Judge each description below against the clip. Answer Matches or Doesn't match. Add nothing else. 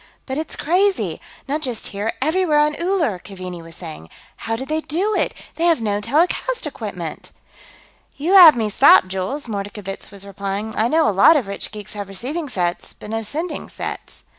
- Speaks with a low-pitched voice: Doesn't match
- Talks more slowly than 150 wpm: Doesn't match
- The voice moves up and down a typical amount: Doesn't match